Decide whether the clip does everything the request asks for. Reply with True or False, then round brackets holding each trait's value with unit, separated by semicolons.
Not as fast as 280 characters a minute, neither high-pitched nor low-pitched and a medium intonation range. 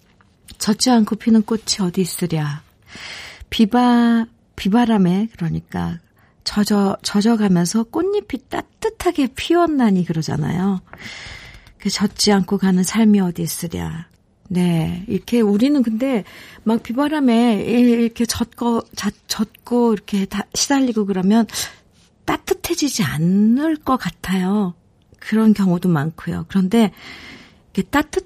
False (250 characters per minute; 210 Hz; 4.4 semitones)